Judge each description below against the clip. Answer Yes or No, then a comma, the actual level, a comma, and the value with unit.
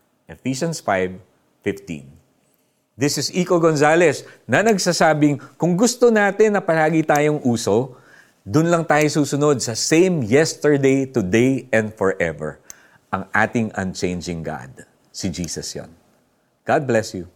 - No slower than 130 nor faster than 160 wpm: No, average, 120 wpm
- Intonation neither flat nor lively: No, wide, 8.1 semitones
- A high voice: No, low, 135 Hz